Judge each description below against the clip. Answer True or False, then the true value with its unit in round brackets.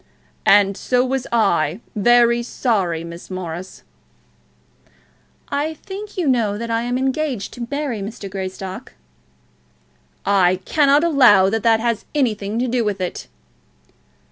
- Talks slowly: True (130 wpm)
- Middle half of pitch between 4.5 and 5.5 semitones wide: True (4.8 semitones)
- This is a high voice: True (230 Hz)